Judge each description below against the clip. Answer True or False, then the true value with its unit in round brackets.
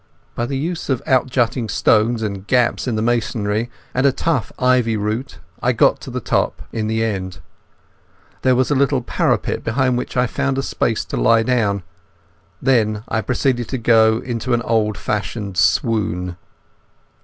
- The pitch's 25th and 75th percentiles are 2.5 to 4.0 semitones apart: True (2.8 semitones)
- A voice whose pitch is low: True (115 Hz)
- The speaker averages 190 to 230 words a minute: False (170 wpm)